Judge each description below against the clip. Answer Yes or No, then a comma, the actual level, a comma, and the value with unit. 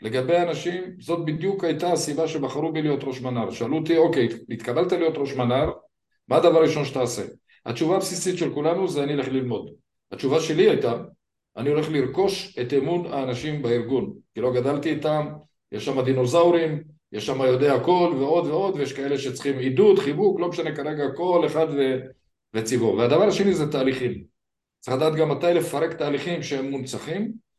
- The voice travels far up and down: No, average, 4.4 semitones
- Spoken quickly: Yes, fast, 170 wpm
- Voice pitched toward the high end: No, medium, 150 Hz